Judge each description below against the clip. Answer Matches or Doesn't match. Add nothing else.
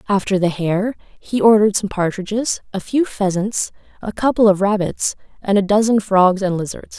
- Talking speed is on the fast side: Doesn't match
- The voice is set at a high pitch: Matches